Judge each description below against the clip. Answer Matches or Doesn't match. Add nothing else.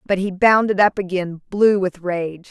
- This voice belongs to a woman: Matches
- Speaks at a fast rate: Doesn't match